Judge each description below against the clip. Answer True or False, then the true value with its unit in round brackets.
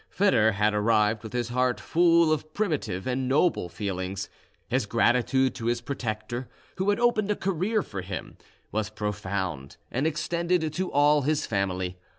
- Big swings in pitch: True (7.4 semitones)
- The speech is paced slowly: False (160 wpm)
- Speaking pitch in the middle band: False (125 Hz)